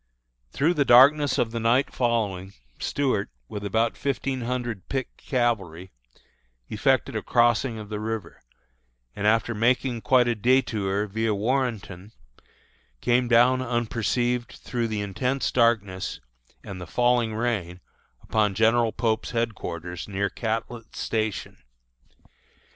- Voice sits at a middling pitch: No, low, 115 Hz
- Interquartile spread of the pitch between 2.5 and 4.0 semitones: Yes, average, 2.9 semitones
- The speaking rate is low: Yes, slow, 120 wpm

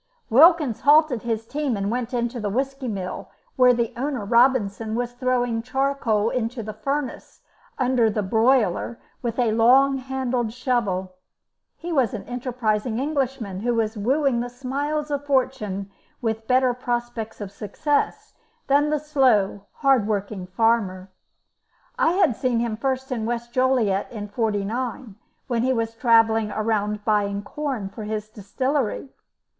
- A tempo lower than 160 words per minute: Yes, average, 145 wpm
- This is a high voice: Yes, high, 240 Hz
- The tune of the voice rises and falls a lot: No, average, 3.5 semitones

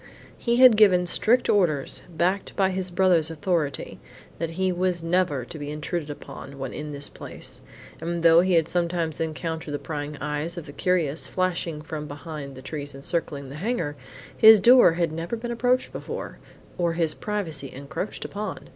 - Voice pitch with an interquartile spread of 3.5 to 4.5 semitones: Yes, average, 3.8 semitones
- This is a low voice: No, medium, 165 Hz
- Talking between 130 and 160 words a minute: No, average, 175 wpm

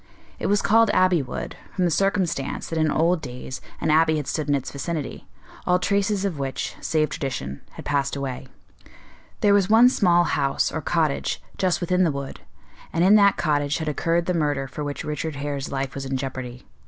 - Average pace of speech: Yes, average, 195 wpm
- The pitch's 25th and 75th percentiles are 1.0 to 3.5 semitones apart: No, average, 4.6 semitones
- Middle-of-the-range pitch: Yes, medium, 155 Hz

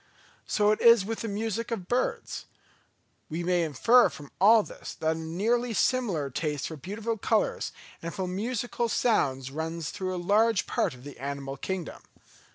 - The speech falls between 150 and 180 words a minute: Yes, average, 165 wpm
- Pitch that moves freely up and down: Yes, wide, 6.1 semitones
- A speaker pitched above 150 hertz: Yes, high, 190 Hz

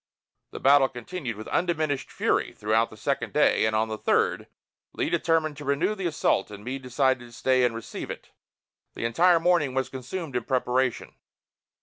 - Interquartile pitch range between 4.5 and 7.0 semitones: Yes, average, 4.9 semitones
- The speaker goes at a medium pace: Yes, average, 180 wpm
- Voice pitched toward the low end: Yes, low, 130 Hz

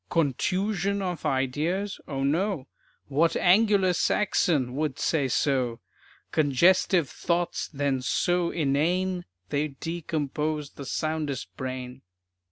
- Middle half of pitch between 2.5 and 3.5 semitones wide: No, average, 4.6 semitones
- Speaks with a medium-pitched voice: Yes, medium, 155 Hz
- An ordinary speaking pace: No, slow, 100 wpm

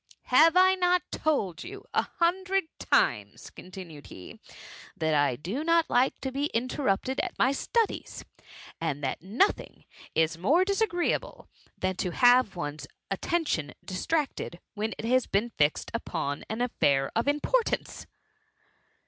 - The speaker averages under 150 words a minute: Yes, average, 140 wpm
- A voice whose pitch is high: Yes, high, 245 Hz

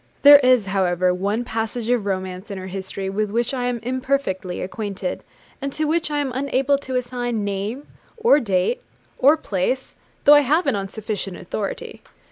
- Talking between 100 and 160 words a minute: No, average, 175 wpm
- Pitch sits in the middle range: No, high, 230 Hz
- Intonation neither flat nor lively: No, wide, 5.7 semitones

